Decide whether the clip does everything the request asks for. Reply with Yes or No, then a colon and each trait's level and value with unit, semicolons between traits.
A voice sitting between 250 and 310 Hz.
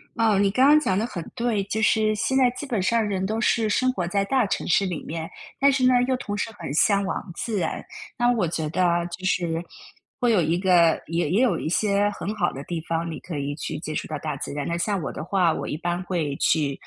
No: medium, 185 Hz